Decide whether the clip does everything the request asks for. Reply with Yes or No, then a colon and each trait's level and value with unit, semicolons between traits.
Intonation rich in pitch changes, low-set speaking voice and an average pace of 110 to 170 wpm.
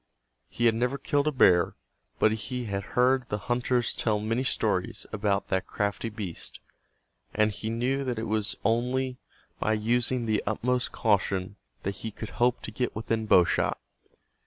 No: average, 3.0 semitones; low, 115 Hz; average, 165 wpm